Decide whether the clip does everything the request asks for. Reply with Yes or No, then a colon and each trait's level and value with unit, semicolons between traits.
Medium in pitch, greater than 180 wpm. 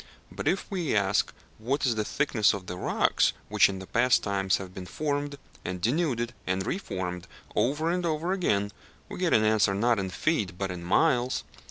No: low, 110 Hz; average, 190 wpm